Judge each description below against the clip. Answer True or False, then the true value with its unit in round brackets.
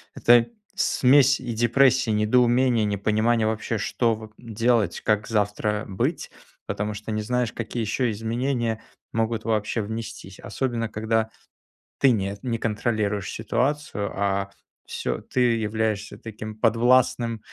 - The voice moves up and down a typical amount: False (2.1 semitones)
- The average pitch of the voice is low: True (110 Hz)